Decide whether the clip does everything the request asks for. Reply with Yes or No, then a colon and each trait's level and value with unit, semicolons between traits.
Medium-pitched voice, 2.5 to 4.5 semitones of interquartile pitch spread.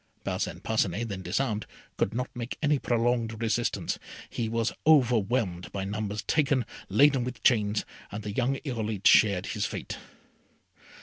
No: low, 115 Hz; average, 3.2 semitones